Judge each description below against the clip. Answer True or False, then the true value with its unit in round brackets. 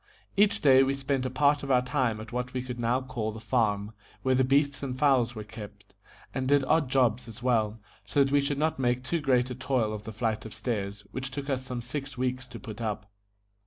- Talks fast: True (235 wpm)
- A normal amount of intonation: True (3.3 semitones)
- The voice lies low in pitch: True (125 Hz)